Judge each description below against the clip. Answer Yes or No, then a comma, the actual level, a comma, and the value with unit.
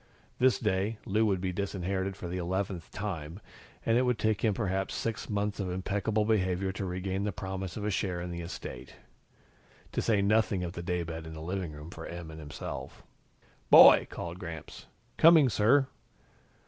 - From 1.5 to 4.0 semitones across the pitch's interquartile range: Yes, average, 3.1 semitones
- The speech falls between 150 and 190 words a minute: Yes, average, 180 wpm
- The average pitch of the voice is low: Yes, very low, 95 Hz